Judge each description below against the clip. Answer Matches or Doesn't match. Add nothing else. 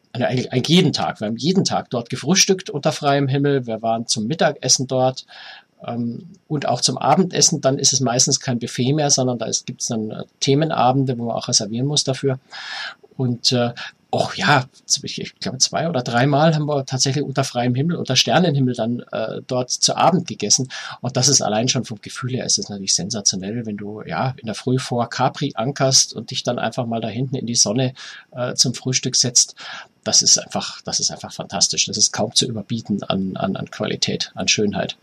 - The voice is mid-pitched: Doesn't match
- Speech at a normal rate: Doesn't match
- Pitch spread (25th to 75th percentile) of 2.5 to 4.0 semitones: Matches